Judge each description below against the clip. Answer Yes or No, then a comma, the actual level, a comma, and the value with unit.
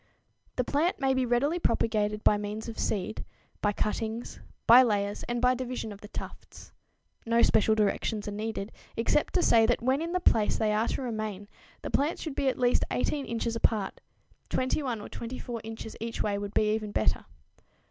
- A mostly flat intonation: No, average, 3.1 semitones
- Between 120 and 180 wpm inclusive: No, average, 190 wpm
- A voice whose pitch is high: Yes, high, 230 Hz